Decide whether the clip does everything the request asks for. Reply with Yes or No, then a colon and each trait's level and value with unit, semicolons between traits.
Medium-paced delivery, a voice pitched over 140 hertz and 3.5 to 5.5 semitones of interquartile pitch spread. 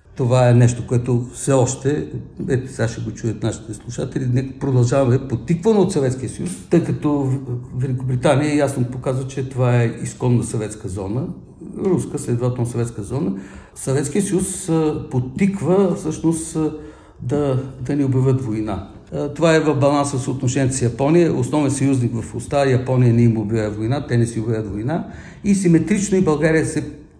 No: average, 155 wpm; low, 130 Hz; average, 4.0 semitones